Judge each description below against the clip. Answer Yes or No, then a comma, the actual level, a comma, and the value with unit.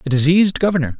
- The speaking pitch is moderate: Yes, medium, 165 Hz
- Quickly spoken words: No, average, 180 wpm